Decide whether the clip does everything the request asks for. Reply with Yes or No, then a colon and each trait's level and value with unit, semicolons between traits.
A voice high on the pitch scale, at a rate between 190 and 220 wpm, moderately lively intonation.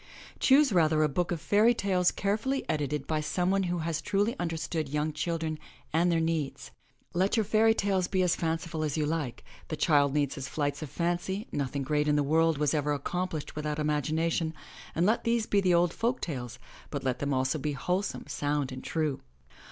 No: medium, 160 Hz; average, 200 wpm; average, 3.6 semitones